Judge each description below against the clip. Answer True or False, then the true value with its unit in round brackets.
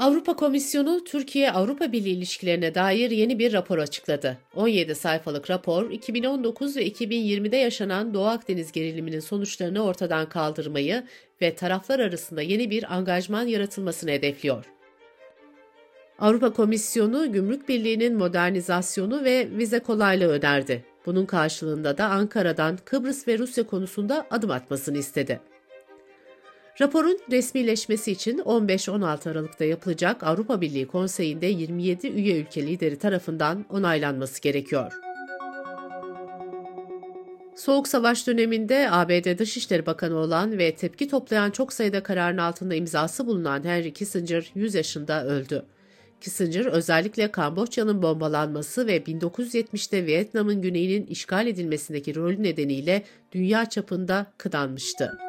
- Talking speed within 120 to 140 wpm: False (110 wpm)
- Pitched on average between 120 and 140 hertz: False (185 Hz)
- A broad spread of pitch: True (5.9 semitones)